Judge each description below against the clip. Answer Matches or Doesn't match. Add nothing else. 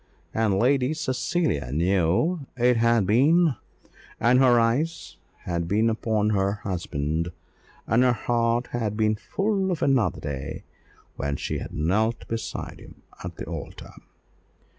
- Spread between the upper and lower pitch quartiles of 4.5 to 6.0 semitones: Matches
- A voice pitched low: Matches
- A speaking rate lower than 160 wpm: Matches